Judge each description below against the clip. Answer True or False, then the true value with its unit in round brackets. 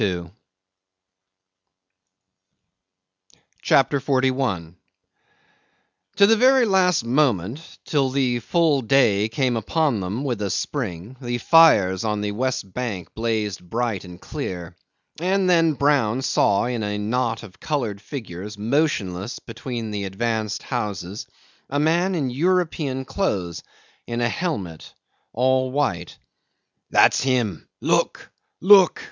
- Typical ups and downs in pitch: False (5.7 semitones)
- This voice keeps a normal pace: False (115 wpm)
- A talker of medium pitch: False (120 Hz)